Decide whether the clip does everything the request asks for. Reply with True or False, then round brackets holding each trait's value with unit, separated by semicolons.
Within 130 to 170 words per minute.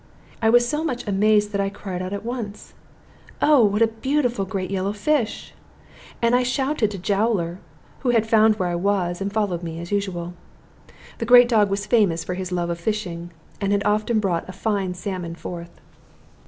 False (190 wpm)